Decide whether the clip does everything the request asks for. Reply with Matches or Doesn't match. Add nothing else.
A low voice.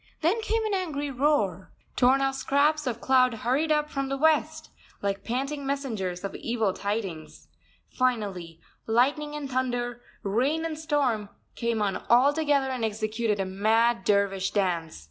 Doesn't match